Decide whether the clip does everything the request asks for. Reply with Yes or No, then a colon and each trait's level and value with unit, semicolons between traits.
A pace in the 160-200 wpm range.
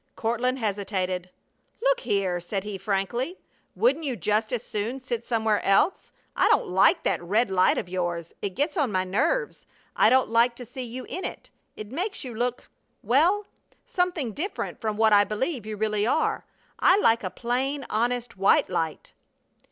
Yes: average, 175 wpm